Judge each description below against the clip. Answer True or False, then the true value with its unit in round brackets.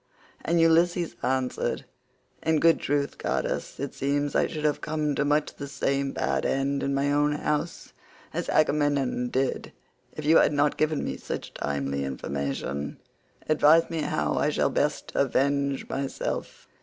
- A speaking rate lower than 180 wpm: True (155 wpm)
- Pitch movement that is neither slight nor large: False (2.2 semitones)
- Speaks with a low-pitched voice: False (145 Hz)